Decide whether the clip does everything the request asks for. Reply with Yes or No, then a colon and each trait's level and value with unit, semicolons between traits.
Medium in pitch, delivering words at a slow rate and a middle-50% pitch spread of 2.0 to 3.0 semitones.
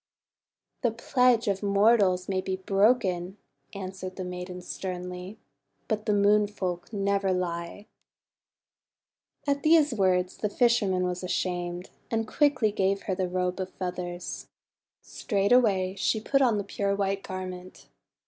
No: high, 195 Hz; slow, 130 wpm; narrow, 2.6 semitones